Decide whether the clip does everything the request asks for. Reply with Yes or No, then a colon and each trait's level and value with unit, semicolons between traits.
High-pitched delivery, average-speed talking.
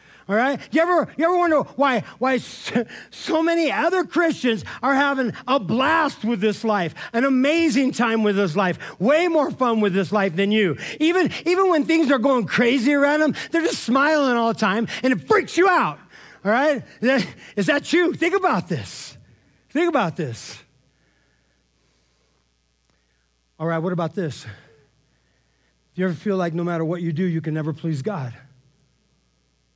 Yes: high, 225 Hz; average, 175 wpm